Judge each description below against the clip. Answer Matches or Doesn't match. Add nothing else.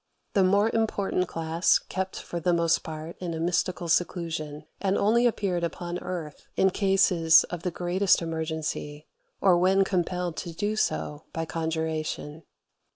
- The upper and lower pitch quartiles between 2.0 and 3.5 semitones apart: Matches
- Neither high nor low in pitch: Matches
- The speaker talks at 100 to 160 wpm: Matches